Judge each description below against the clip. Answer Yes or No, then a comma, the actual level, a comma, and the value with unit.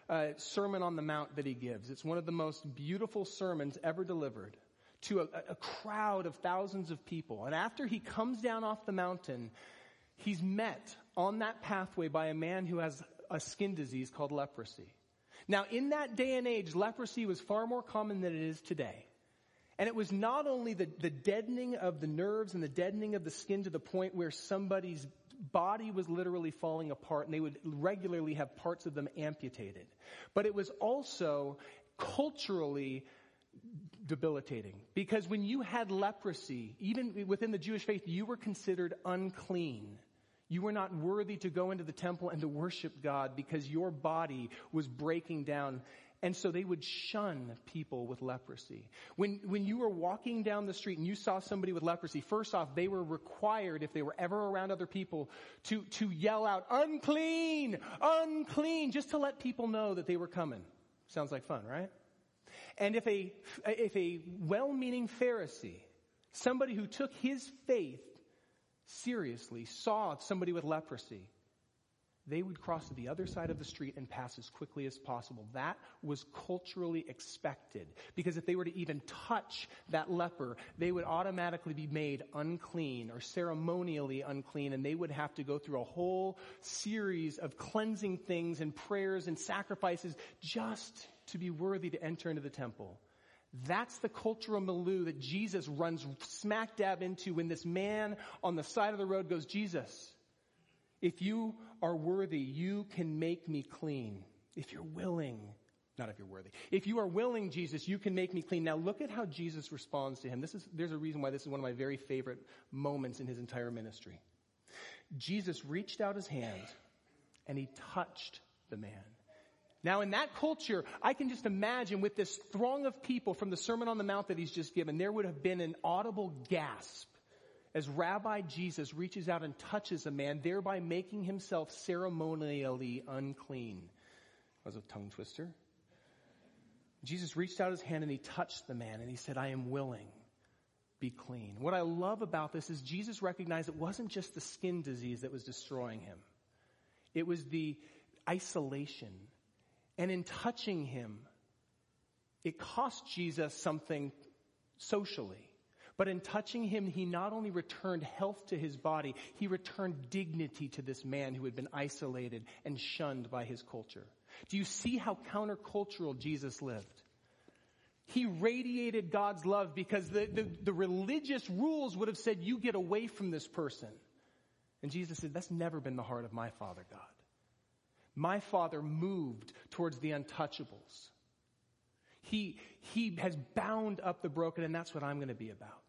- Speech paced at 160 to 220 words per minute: Yes, average, 175 wpm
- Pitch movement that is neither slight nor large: No, wide, 6.0 semitones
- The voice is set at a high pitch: No, medium, 170 Hz